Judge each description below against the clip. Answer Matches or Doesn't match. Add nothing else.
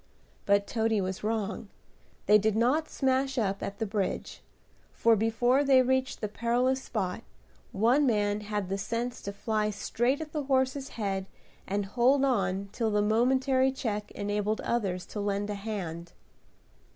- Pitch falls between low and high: Doesn't match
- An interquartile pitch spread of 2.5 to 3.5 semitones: Doesn't match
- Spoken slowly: Doesn't match